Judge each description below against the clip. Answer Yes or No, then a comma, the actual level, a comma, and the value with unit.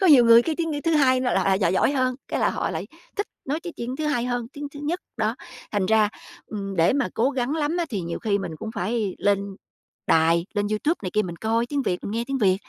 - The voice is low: No, high, 230 Hz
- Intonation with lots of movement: Yes, wide, 6.2 semitones